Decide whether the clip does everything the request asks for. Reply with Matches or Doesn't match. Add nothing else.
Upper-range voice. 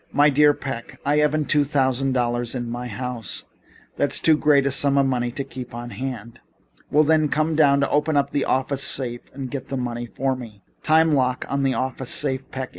Doesn't match